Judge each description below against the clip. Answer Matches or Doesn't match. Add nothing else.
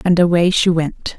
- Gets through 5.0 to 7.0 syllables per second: Doesn't match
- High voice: Doesn't match